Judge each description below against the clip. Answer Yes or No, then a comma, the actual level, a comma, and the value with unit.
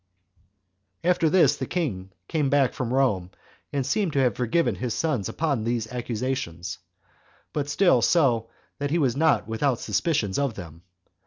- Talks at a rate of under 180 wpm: Yes, average, 165 wpm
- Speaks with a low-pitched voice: Yes, low, 130 Hz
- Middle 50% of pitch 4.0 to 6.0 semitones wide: Yes, average, 5.1 semitones